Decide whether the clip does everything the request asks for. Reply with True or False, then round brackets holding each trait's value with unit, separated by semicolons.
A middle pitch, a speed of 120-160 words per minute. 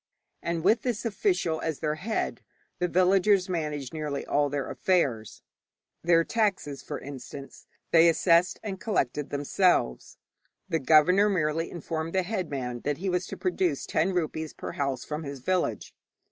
True (165 Hz; 150 wpm)